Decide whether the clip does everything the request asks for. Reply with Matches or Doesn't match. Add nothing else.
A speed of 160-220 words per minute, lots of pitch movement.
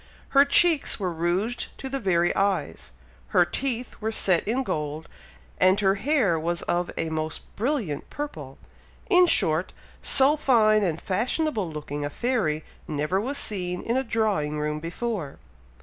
Doesn't match